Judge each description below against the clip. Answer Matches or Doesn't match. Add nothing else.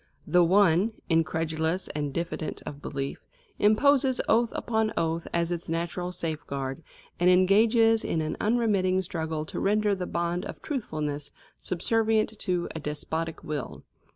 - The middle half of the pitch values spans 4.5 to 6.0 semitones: Matches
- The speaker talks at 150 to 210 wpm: Doesn't match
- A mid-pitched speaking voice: Matches